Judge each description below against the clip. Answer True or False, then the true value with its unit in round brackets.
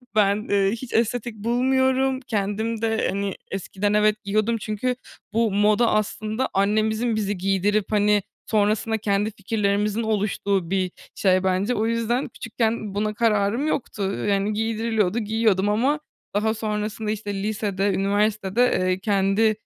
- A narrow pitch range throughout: True (2.0 semitones)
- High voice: True (215 Hz)